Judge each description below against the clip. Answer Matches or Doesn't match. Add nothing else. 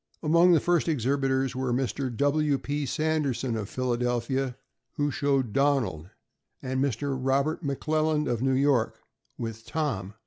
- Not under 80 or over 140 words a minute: Matches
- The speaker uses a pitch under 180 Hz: Matches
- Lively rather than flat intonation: Doesn't match